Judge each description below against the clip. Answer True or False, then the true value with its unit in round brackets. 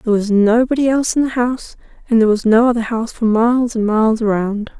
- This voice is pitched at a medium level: False (230 Hz)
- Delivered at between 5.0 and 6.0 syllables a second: False (6.6 syllables/s)